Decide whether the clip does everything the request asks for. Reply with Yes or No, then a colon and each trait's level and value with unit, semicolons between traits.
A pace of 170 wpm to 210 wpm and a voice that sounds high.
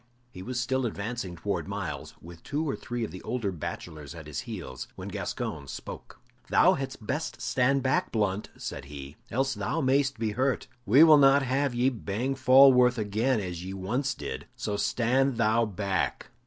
No: average, 180 wpm; low, 115 Hz